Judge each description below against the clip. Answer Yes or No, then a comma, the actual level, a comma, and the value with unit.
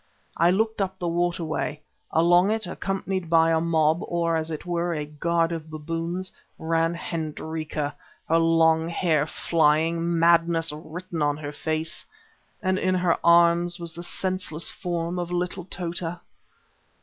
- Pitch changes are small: Yes, narrow, 1.6 semitones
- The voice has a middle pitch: Yes, medium, 170 Hz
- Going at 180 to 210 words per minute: No, average, 150 wpm